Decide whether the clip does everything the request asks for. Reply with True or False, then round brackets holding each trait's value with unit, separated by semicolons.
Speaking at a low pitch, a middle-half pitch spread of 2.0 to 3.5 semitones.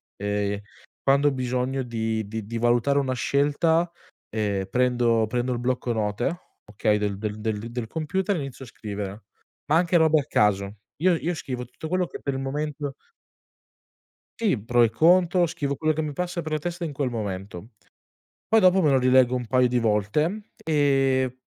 False (130 Hz; 5.6 semitones)